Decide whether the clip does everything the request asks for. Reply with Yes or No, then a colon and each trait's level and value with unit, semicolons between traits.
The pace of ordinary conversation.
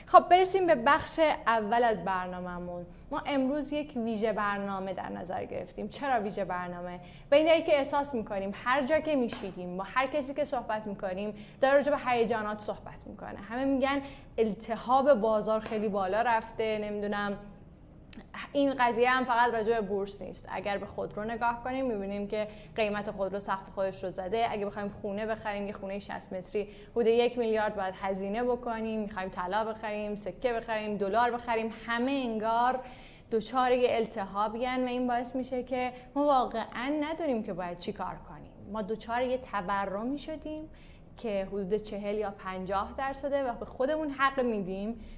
No: fast, 165 wpm